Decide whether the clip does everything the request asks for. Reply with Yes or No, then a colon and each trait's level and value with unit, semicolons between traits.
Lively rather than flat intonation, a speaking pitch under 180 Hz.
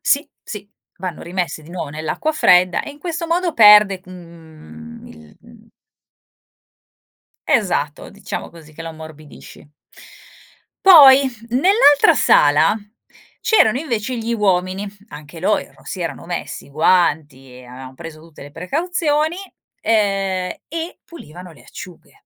No: wide, 8.9 semitones; medium, 185 Hz